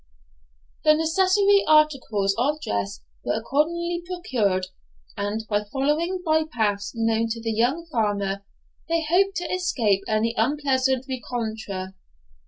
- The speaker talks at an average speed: No, slow, 120 wpm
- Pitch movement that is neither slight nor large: No, wide, 6.9 semitones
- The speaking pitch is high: Yes, very high, 255 Hz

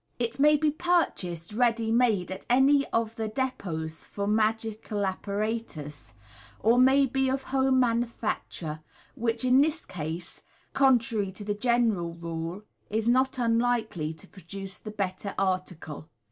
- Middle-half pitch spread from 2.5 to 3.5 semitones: No, average, 5.2 semitones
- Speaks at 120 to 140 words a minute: Yes, slow, 135 wpm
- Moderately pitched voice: No, high, 220 Hz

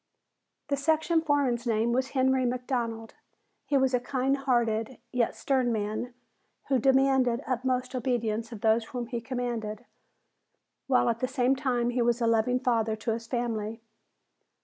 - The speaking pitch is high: Yes, high, 245 Hz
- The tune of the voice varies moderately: No, narrow, 2.3 semitones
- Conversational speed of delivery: Yes, average, 150 wpm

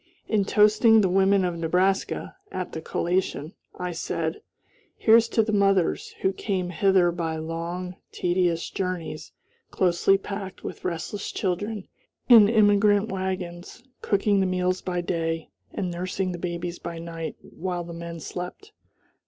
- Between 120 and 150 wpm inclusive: Yes, average, 140 wpm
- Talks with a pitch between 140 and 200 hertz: Yes, medium, 185 Hz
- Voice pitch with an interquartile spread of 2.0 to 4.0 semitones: Yes, narrow, 2.4 semitones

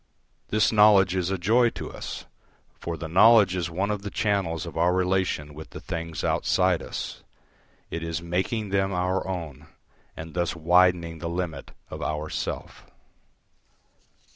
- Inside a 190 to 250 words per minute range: No, average, 155 wpm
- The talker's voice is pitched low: Yes, very low, 90 Hz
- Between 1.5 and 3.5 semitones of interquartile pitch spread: Yes, average, 2.8 semitones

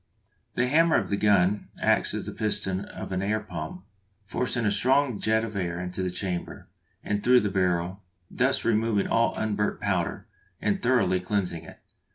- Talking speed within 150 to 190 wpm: Yes, average, 175 wpm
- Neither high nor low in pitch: No, low, 105 Hz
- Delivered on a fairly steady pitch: No, average, 3.4 semitones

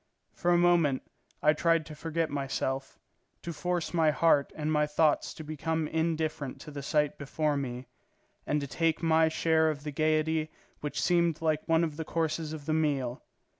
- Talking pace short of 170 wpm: No, average, 180 wpm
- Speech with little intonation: Yes, narrow, 1.7 semitones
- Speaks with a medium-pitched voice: Yes, medium, 155 Hz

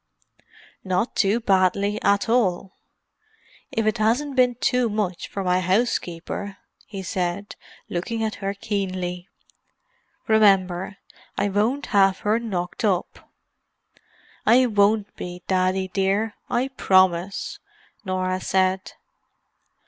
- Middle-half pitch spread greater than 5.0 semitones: No, average, 2.9 semitones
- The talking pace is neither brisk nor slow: No, slow, 105 wpm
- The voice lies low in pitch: No, high, 200 Hz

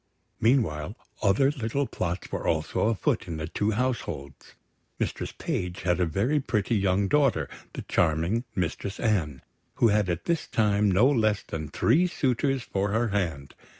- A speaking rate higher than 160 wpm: No, average, 150 wpm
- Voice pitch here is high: No, low, 100 Hz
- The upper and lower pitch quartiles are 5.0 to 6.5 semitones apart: Yes, wide, 5.5 semitones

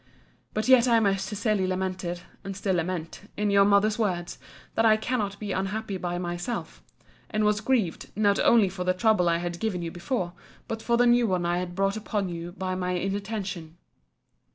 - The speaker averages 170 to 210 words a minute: Yes, average, 190 wpm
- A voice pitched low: No, high, 195 Hz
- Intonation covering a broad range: No, average, 3.2 semitones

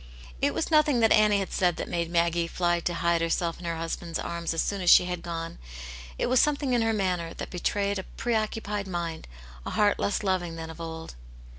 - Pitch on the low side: No, medium, 180 Hz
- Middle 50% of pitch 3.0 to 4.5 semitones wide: Yes, average, 3.6 semitones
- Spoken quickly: Yes, fast, 220 wpm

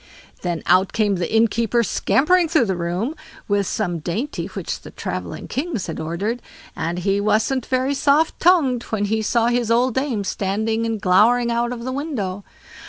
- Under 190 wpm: Yes, average, 170 wpm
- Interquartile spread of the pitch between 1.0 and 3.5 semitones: No, average, 4.5 semitones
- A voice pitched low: No, high, 225 Hz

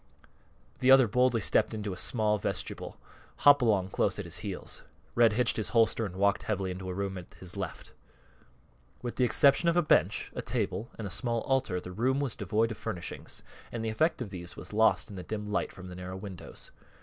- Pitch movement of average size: Yes, average, 4.3 semitones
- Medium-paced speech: No, fast, 210 wpm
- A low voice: Yes, low, 105 Hz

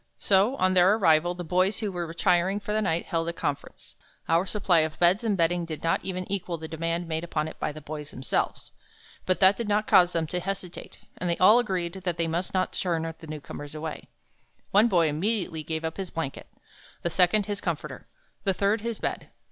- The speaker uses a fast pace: Yes, fast, 210 wpm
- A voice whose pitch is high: No, medium, 175 Hz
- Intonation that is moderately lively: Yes, average, 3.0 semitones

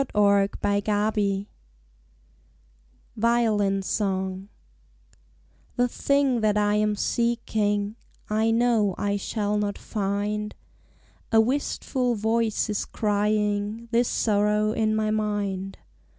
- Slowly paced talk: Yes, slow, 95 wpm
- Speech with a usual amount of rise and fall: No, narrow, 1.6 semitones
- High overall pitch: Yes, high, 210 Hz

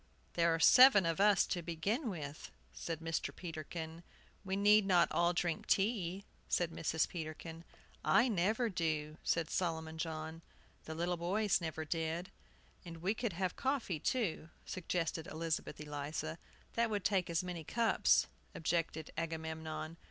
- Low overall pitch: No, medium, 170 Hz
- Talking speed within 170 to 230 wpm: No, average, 145 wpm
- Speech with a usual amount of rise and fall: Yes, average, 3.1 semitones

